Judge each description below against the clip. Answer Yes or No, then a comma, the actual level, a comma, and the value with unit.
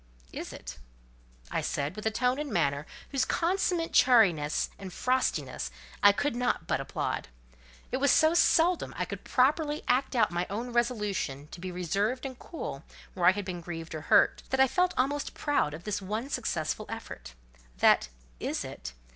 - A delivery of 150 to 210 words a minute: Yes, average, 175 wpm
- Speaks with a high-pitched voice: Yes, high, 220 Hz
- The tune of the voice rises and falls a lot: Yes, wide, 7.3 semitones